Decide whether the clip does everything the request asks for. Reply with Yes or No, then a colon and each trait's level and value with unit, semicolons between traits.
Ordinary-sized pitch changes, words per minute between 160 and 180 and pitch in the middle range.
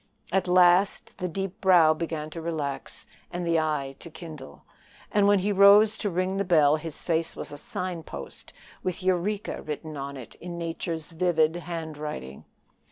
Yes: average, 3.0 semitones; average, 165 wpm; medium, 170 Hz